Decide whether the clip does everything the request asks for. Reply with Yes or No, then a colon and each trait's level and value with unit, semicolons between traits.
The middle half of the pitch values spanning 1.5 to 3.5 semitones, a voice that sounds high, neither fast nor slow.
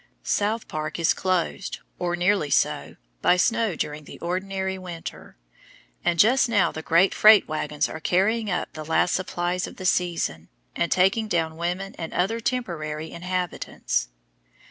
No: average, 3.1 semitones; medium, 180 Hz; average, 150 wpm